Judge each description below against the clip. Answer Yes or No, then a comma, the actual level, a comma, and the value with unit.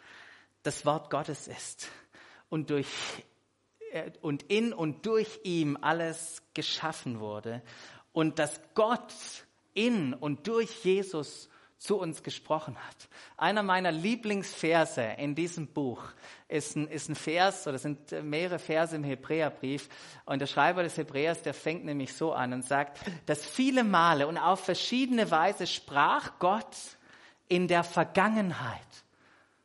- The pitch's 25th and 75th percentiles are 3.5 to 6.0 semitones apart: Yes, average, 4.0 semitones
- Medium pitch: Yes, medium, 160 Hz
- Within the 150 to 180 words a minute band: No, average, 135 wpm